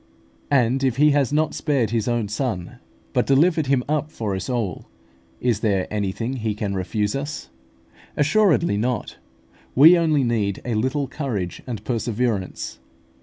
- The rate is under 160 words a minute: Yes, average, 150 wpm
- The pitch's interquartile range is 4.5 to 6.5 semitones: Yes, average, 5.0 semitones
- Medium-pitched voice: No, low, 120 Hz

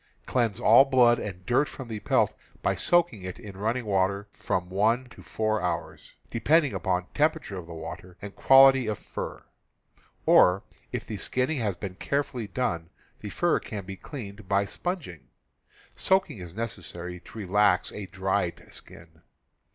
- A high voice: No, low, 105 Hz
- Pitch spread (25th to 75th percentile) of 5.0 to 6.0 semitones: Yes, average, 5.3 semitones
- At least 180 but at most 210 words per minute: No, average, 155 wpm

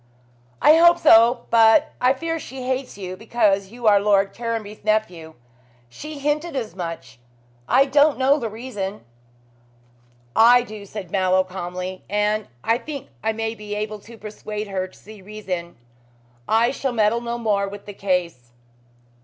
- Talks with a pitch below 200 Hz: No, high, 215 Hz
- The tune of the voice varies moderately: Yes, average, 3.8 semitones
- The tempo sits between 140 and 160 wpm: Yes, average, 155 wpm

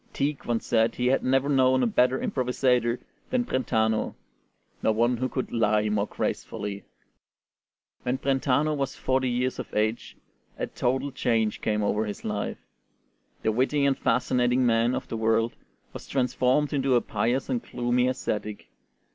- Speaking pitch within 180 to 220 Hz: No, low, 125 Hz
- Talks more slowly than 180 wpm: Yes, average, 155 wpm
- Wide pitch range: No, average, 2.8 semitones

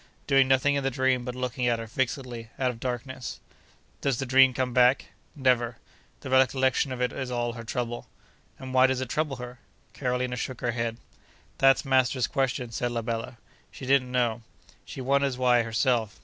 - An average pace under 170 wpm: No, average, 185 wpm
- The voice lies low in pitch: Yes, low, 125 Hz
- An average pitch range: No, narrow, 1.5 semitones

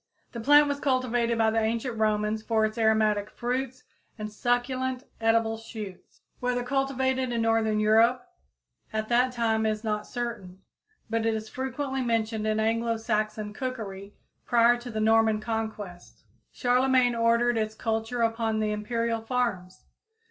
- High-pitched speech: Yes, high, 225 Hz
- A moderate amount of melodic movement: No, narrow, 2.1 semitones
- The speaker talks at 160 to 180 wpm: No, average, 145 wpm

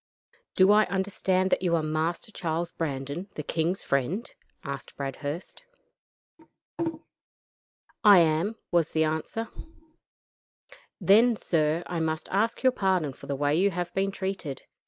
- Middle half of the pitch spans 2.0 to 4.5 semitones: Yes, average, 3.8 semitones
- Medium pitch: Yes, medium, 170 Hz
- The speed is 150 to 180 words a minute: No, slow, 135 wpm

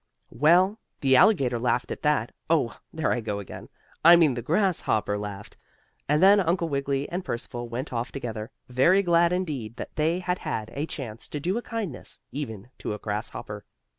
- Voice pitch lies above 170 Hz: No, medium, 140 Hz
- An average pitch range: No, wide, 6.6 semitones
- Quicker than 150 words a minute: Yes, average, 180 wpm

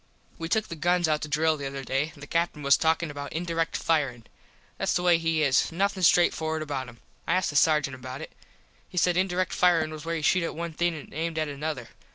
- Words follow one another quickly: Yes, fast, 235 wpm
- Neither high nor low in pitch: Yes, medium, 160 Hz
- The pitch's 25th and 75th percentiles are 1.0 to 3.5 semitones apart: Yes, average, 2.7 semitones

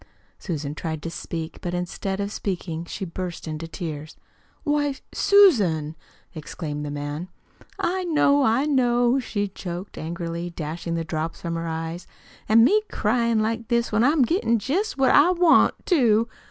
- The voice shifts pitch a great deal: Yes, wide, 7.1 semitones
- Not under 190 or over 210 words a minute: No, average, 155 wpm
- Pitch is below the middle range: No, high, 190 Hz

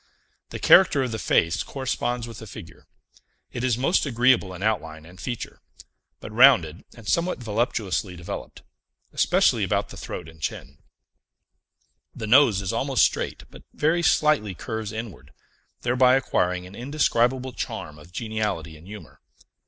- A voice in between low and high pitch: No, low, 110 Hz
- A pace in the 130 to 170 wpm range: Yes, average, 145 wpm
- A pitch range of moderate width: No, wide, 5.8 semitones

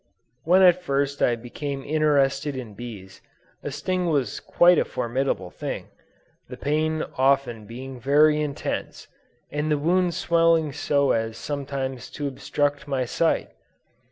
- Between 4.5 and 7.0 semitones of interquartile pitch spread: No, average, 3.1 semitones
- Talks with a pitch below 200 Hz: Yes, medium, 140 Hz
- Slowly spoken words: Yes, slow, 130 wpm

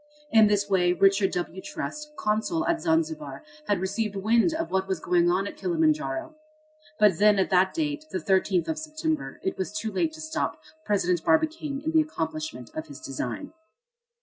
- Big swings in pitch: Yes, wide, 8.8 semitones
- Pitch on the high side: Yes, high, 210 Hz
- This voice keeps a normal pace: Yes, average, 175 wpm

